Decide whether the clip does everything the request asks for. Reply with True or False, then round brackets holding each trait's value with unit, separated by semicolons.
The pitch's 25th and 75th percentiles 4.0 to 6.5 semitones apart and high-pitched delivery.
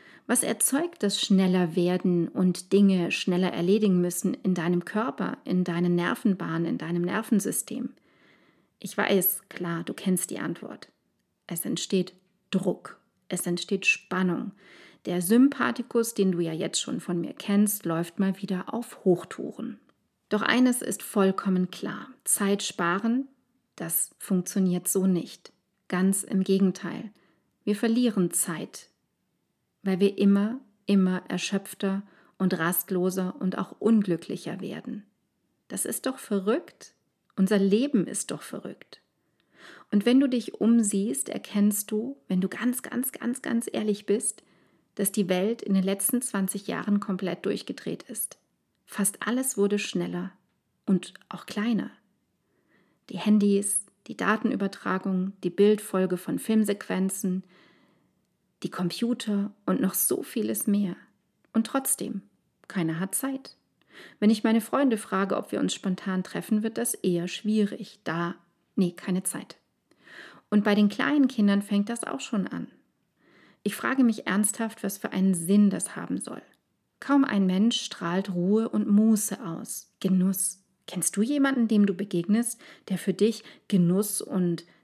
False (3.2 semitones; 200 Hz)